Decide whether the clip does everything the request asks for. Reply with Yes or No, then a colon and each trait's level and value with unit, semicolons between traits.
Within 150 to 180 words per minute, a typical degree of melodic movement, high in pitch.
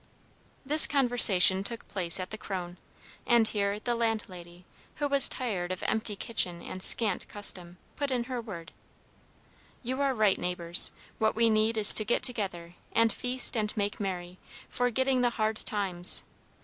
Yes: average, 160 wpm; average, 4.4 semitones; high, 215 Hz